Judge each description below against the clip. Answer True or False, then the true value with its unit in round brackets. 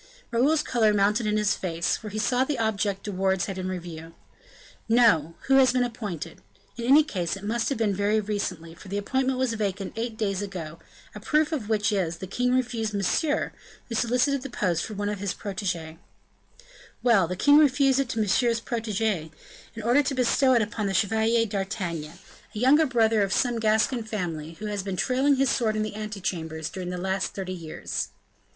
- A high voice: True (215 Hz)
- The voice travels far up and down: False (4.1 semitones)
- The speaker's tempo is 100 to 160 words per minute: False (200 wpm)